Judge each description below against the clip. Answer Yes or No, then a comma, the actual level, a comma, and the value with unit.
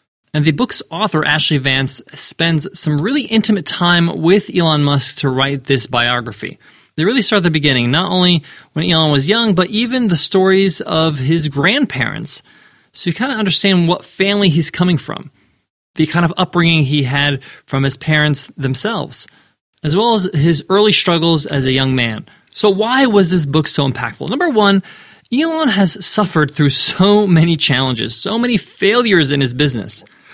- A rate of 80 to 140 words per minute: No, average, 175 wpm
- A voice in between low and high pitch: Yes, medium, 165 Hz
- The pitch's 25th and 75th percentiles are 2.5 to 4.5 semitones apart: No, wide, 5.5 semitones